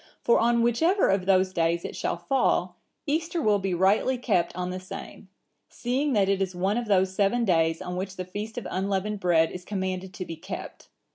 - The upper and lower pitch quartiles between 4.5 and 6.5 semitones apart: No, average, 4.0 semitones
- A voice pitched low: No, high, 190 Hz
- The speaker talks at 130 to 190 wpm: No, fast, 205 wpm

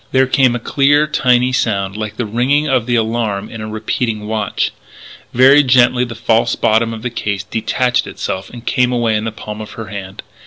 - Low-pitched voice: Yes, low, 115 Hz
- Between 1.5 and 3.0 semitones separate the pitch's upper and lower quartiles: Yes, narrow, 2.6 semitones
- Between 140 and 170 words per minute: No, average, 200 wpm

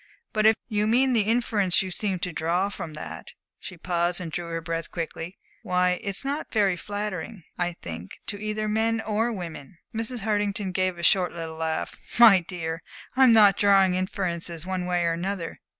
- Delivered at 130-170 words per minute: No, average, 180 wpm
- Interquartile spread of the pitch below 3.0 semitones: No, average, 3.7 semitones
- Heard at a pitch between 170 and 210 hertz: Yes, medium, 185 Hz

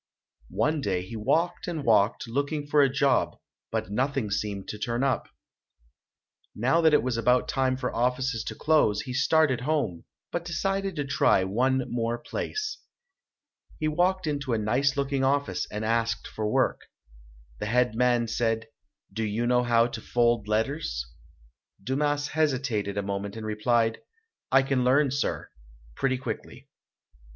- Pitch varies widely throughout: No, average, 4.1 semitones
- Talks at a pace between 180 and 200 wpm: No, average, 155 wpm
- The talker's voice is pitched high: No, low, 125 Hz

